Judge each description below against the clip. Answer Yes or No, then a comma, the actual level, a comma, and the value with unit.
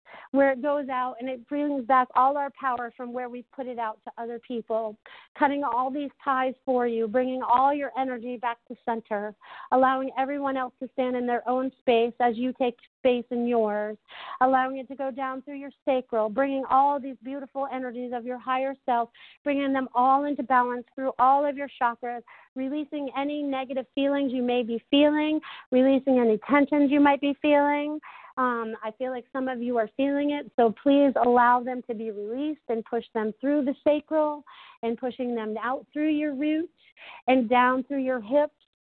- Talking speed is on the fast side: No, average, 195 wpm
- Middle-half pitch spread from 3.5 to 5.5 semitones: No, narrow, 2.4 semitones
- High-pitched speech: Yes, very high, 260 Hz